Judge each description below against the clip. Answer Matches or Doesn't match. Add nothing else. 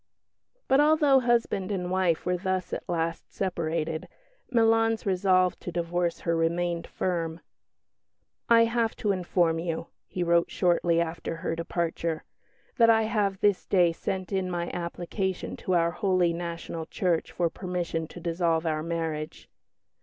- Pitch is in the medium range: Matches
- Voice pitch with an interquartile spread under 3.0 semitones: Matches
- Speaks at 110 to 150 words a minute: Matches